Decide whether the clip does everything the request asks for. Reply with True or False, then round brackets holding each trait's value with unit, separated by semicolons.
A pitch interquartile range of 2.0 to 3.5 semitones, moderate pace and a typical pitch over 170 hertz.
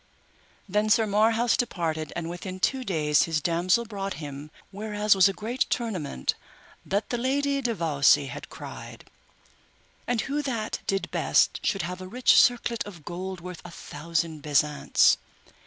False (5.5 semitones; 155 wpm; 190 Hz)